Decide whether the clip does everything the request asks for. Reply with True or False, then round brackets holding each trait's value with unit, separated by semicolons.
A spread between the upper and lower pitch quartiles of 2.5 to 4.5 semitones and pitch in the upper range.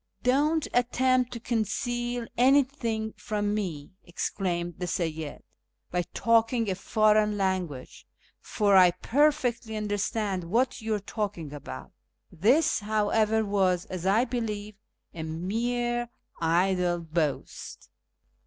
False (4.9 semitones; 210 Hz)